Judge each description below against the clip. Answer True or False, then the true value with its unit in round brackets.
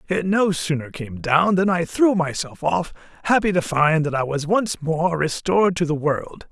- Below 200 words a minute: False (205 wpm)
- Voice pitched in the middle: True (165 Hz)